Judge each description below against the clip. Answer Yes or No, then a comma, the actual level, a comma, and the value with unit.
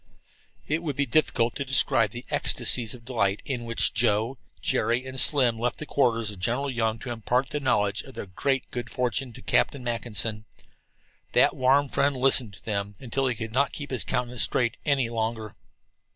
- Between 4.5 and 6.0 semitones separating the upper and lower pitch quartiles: No, average, 2.9 semitones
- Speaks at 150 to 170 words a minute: No, average, 185 wpm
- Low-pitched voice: Yes, low, 120 Hz